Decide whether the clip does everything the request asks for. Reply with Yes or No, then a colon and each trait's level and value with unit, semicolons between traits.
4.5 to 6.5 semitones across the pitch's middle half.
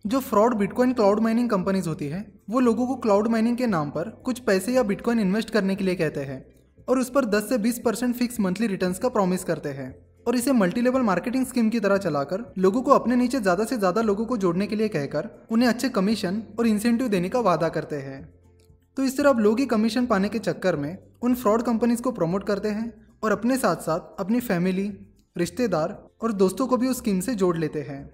Yes: average, 4.8 semitones